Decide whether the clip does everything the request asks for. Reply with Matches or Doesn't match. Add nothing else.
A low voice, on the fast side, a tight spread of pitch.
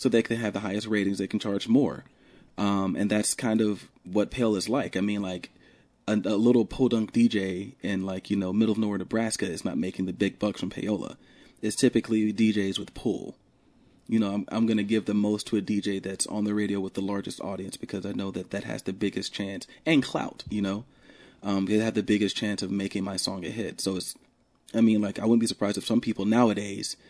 Matches